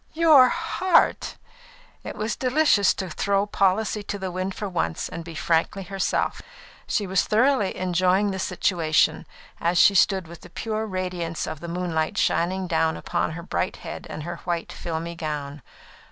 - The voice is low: No, medium, 185 Hz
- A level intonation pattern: No, average, 3.2 semitones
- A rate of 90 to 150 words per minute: No, average, 165 wpm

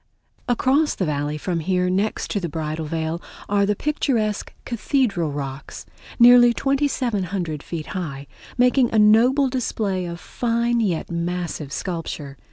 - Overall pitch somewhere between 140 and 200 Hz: Yes, high, 190 Hz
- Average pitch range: No, wide, 6.5 semitones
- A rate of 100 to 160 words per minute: Yes, slow, 135 wpm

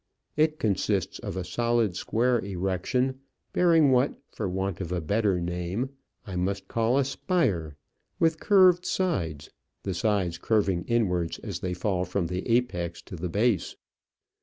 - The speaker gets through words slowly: No, average, 150 wpm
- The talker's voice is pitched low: Yes, low, 100 Hz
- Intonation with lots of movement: Yes, wide, 5.8 semitones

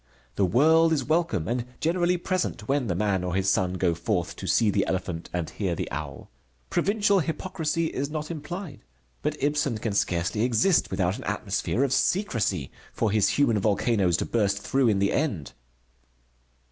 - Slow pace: No, average, 170 wpm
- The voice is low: Yes, low, 115 Hz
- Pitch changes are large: Yes, wide, 8.6 semitones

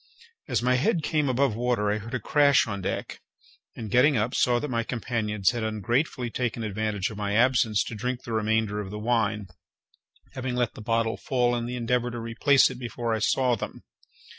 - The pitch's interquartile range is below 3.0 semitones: Yes, narrow, 2.5 semitones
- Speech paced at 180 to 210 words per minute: Yes, fast, 205 wpm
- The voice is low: Yes, low, 115 Hz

